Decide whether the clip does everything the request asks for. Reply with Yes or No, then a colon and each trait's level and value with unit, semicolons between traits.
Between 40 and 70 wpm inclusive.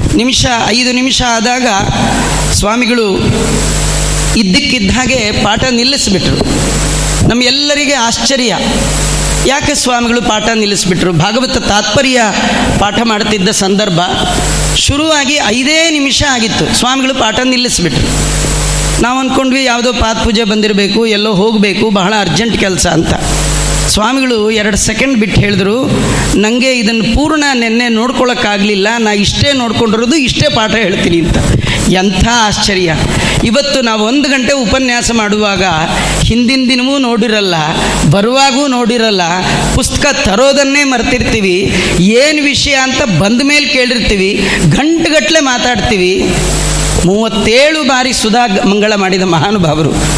No: average, 100 wpm